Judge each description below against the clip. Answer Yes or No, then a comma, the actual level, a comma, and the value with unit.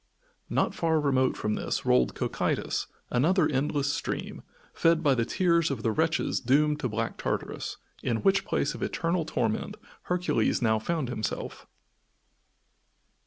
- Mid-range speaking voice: Yes, medium, 145 Hz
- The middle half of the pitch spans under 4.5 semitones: No, wide, 5.6 semitones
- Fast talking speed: No, average, 140 wpm